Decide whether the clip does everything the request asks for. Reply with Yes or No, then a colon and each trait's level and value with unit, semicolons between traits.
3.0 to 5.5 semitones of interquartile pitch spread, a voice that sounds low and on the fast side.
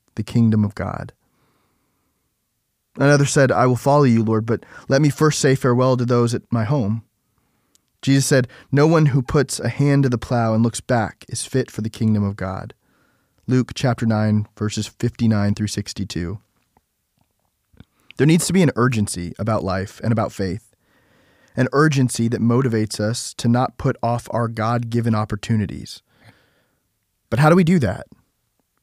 No: average, 3.5 semitones; low, 120 Hz; average, 165 wpm